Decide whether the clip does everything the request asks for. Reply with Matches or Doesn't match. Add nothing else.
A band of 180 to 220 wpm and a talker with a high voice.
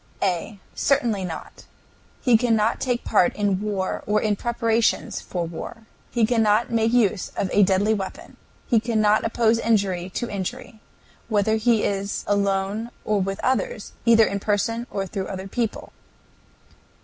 Doesn't match